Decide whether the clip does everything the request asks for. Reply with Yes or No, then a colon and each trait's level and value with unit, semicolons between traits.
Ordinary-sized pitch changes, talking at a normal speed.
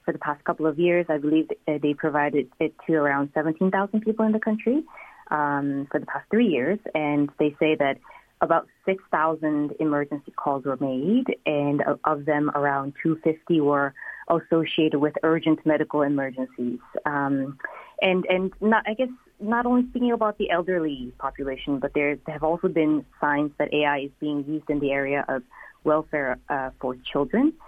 Yes: average, 3.4 semitones; average, 165 wpm